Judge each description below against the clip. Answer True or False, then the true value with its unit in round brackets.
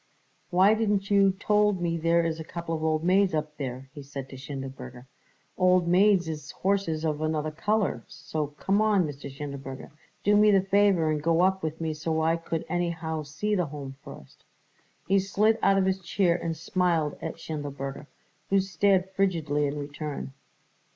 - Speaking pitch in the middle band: True (165 Hz)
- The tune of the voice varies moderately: True (4.3 semitones)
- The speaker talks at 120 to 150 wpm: False (175 wpm)